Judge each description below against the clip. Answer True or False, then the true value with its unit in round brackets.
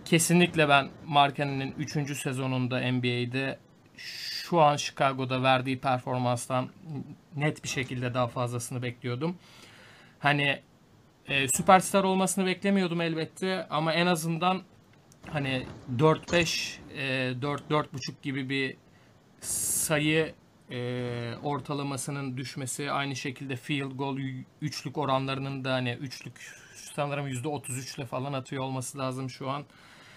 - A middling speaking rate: True (105 wpm)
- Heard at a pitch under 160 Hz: True (140 Hz)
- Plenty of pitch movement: False (2.7 semitones)